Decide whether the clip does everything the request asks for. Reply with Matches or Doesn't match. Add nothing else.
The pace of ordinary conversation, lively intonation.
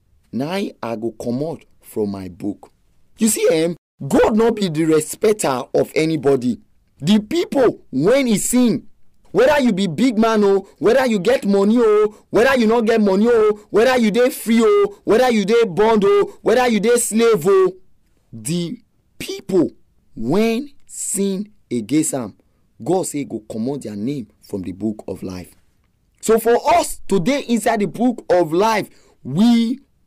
Matches